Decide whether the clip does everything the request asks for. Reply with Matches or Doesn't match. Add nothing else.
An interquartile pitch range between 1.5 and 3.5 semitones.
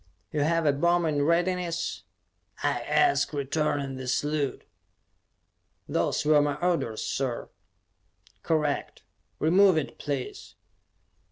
Matches